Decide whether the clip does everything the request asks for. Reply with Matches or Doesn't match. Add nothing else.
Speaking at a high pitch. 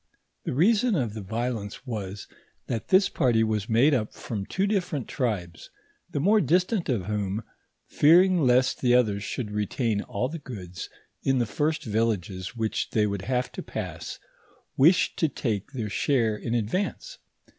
Doesn't match